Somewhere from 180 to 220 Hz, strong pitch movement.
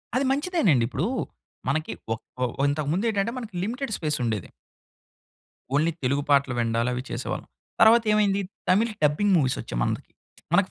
No: medium, 155 Hz; wide, 8.7 semitones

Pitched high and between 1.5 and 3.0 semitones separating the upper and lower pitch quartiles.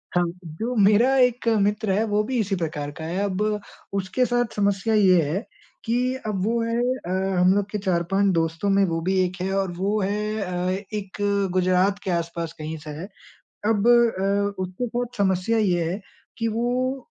No: high, 200 Hz; average, 3.5 semitones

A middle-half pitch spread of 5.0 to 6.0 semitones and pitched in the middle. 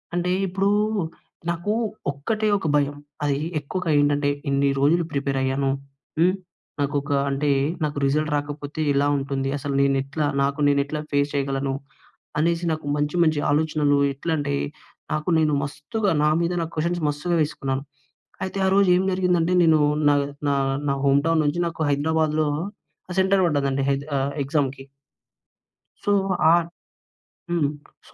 No: average, 2.9 semitones; medium, 145 Hz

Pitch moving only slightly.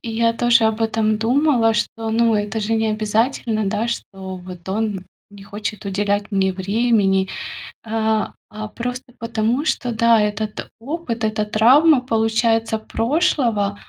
Yes: narrow, 2.0 semitones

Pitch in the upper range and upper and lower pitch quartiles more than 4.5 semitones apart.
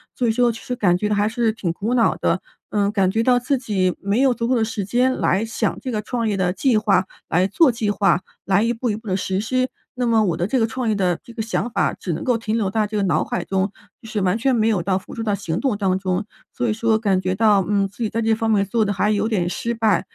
No: high, 215 Hz; average, 3.0 semitones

